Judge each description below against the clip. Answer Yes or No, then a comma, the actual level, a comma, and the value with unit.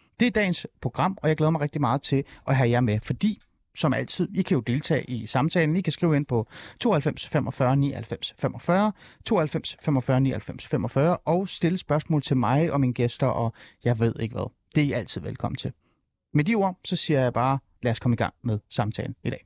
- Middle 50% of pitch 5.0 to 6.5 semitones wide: Yes, average, 5.3 semitones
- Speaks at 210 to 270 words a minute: Yes, average, 220 wpm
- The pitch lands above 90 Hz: Yes, medium, 140 Hz